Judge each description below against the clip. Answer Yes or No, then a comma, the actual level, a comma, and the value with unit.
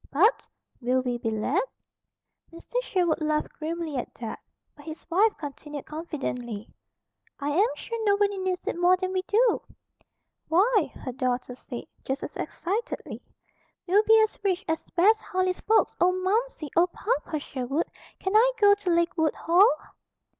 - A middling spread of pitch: No, wide, 5.7 semitones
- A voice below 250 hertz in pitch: No, very high, 345 Hz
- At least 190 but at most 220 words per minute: No, average, 155 wpm